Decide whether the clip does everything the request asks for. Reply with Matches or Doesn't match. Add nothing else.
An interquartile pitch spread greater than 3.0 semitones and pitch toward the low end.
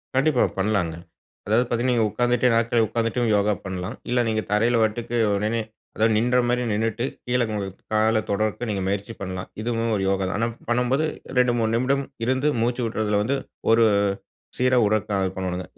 Doesn't match